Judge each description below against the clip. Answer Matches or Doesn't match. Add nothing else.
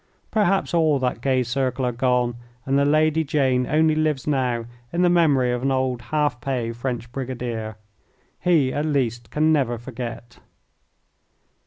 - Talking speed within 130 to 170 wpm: Matches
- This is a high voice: Doesn't match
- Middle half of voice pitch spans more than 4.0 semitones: Doesn't match